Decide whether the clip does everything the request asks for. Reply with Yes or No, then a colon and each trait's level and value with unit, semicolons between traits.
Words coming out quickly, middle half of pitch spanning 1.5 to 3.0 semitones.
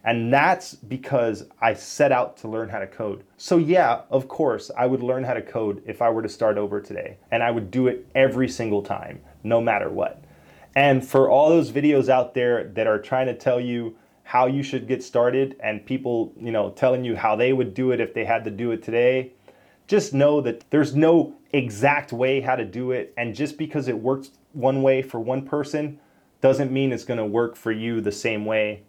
Yes: fast, 220 wpm; average, 2.7 semitones